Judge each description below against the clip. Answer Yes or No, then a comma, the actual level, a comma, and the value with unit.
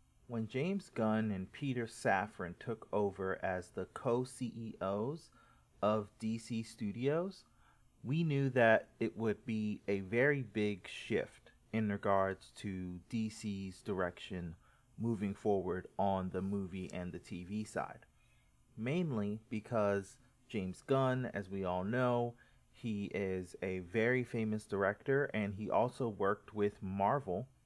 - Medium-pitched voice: No, low, 110 Hz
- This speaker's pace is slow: Yes, slow, 130 wpm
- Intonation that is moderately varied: Yes, average, 3.3 semitones